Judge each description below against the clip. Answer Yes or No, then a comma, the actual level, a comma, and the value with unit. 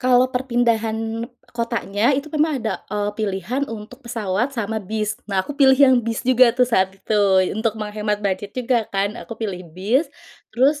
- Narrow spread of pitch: No, average, 3.3 semitones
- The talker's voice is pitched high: Yes, high, 225 Hz